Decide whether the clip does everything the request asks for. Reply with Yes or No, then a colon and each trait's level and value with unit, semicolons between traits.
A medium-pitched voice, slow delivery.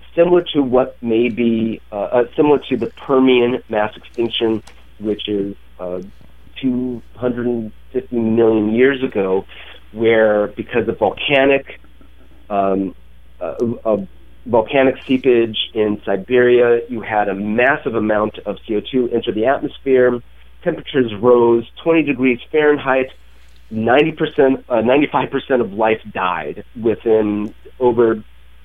No: low, 115 Hz; slow, 115 wpm